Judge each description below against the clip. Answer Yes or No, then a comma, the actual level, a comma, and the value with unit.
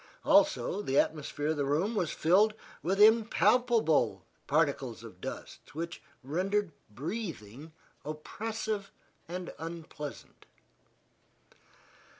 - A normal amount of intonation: No, wide, 5.9 semitones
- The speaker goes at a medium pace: No, slow, 95 wpm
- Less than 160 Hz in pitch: No, medium, 175 Hz